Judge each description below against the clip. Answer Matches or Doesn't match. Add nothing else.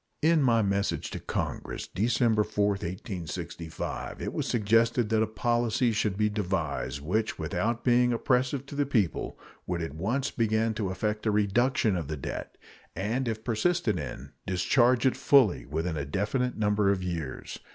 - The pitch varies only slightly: Doesn't match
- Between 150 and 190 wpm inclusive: Matches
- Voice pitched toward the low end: Matches